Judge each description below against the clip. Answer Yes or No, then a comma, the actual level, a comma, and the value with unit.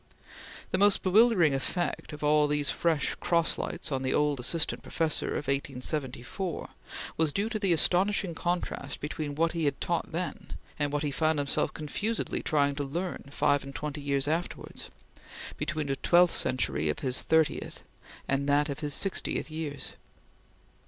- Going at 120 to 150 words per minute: No, average, 160 wpm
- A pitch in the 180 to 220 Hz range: No, medium, 150 Hz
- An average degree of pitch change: Yes, average, 3.3 semitones